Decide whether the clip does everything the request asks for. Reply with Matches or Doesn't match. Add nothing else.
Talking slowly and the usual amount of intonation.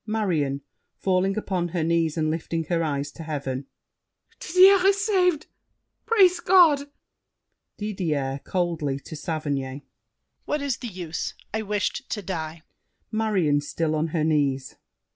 Doesn't match